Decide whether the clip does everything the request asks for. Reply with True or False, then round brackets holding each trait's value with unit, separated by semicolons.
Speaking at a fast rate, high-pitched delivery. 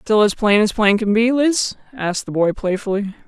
True (220 wpm; 215 Hz)